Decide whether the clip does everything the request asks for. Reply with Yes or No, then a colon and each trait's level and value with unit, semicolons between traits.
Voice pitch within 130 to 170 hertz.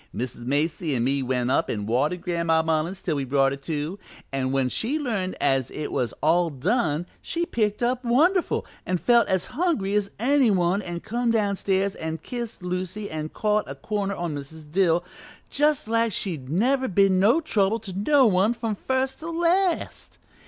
No: high, 190 Hz